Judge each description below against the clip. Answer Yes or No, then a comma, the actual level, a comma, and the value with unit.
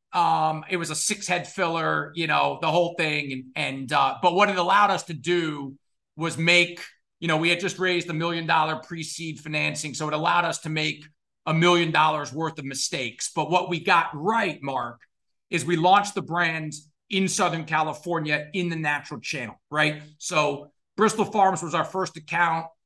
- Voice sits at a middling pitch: Yes, medium, 165 Hz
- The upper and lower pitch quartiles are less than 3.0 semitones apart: Yes, narrow, 2.5 semitones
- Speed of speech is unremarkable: Yes, average, 195 wpm